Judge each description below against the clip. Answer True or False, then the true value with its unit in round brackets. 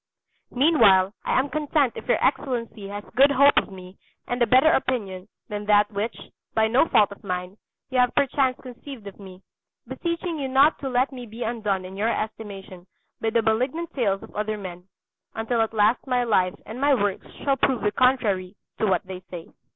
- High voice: True (225 Hz)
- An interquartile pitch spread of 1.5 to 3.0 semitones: False (4.6 semitones)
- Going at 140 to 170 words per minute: False (195 wpm)